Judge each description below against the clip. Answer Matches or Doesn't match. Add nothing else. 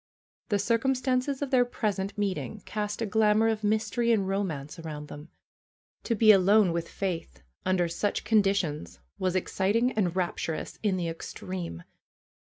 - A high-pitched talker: Matches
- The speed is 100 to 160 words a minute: Matches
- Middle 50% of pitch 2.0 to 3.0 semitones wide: Doesn't match